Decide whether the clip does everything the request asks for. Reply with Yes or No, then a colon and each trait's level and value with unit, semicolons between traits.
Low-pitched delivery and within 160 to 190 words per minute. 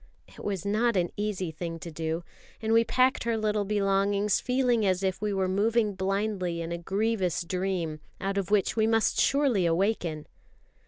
No: high, 195 Hz; average, 175 wpm